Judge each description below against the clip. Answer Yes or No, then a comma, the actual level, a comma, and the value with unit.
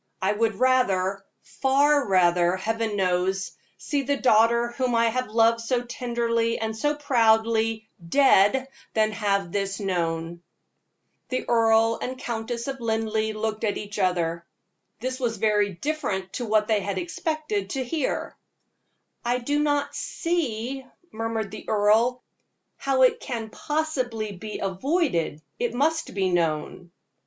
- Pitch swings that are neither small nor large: Yes, average, 4.1 semitones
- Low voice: No, high, 225 Hz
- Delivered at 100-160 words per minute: Yes, slow, 135 wpm